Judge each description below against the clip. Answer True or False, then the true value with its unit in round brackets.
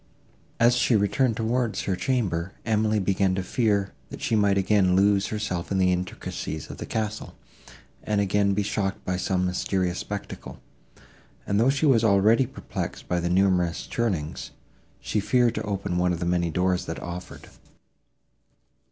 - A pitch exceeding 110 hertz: False (100 Hz)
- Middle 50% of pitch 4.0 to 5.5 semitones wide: False (3.1 semitones)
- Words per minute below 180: True (160 wpm)